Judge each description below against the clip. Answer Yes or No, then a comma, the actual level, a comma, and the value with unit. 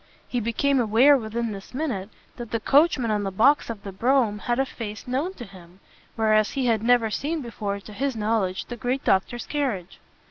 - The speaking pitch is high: Yes, high, 230 Hz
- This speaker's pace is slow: No, average, 200 wpm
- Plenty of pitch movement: No, average, 4.0 semitones